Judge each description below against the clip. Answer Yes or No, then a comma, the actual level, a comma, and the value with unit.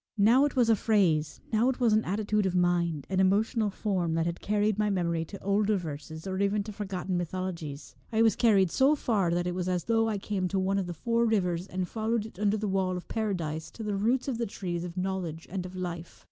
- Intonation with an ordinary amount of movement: Yes, average, 3.4 semitones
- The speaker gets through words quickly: Yes, fast, 240 wpm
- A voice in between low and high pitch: No, high, 195 Hz